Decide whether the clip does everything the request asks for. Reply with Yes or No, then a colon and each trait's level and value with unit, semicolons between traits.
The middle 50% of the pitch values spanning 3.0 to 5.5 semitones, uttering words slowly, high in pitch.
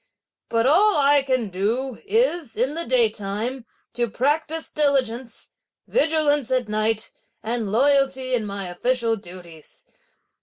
Yes: average, 4.6 semitones; slow, 120 wpm; very high, 250 Hz